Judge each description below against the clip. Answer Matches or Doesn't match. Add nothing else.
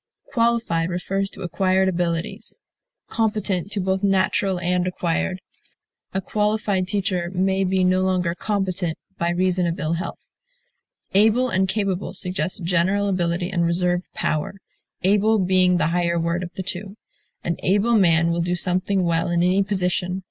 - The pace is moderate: Matches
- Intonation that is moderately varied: Doesn't match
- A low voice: Doesn't match